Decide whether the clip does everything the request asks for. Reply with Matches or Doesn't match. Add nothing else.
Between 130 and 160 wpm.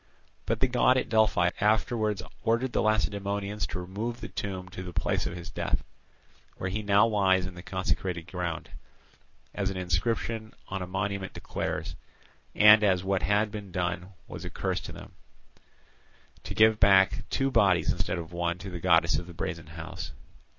Doesn't match